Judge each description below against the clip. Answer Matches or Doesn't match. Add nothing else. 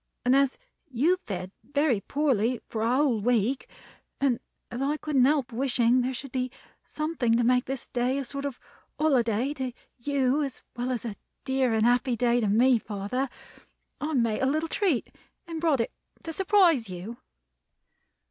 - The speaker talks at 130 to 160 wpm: Doesn't match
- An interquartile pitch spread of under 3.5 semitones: Matches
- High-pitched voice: Matches